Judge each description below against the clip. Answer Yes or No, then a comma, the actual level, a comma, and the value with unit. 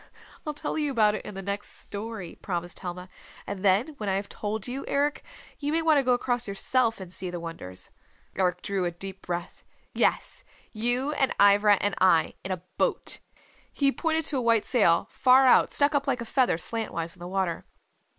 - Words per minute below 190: No, average, 200 wpm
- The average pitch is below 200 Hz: No, high, 210 Hz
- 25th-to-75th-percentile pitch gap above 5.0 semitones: Yes, wide, 5.6 semitones